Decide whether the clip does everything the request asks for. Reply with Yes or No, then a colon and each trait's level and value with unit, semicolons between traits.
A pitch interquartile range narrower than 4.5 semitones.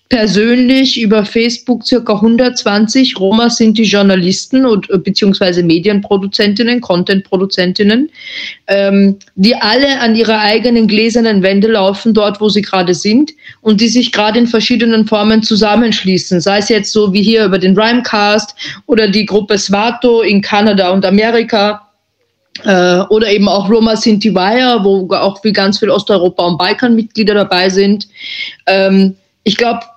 Yes: average, 2.7 semitones